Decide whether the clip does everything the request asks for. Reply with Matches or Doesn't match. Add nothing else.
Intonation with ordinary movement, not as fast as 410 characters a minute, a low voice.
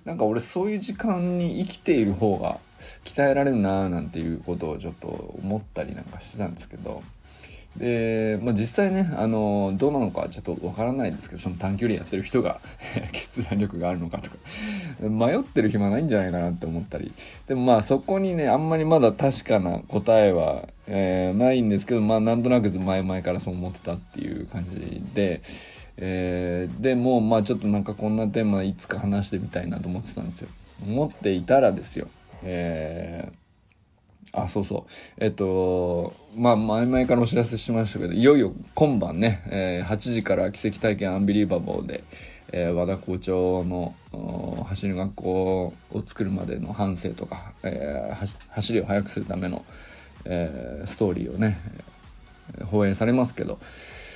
Matches